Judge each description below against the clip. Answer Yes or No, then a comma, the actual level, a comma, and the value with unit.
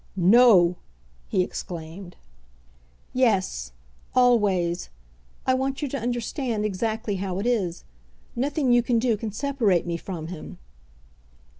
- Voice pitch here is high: Yes, high, 215 Hz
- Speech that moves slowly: Yes, slow, 120 wpm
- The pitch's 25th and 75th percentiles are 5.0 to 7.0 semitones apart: Yes, average, 5.3 semitones